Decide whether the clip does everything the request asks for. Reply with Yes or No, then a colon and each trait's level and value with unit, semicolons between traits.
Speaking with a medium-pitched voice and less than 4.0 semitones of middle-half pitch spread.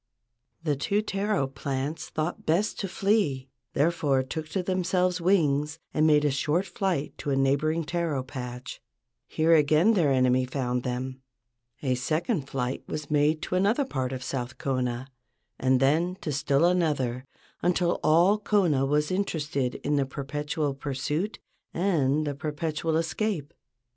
No: medium, 150 Hz; average, 4.4 semitones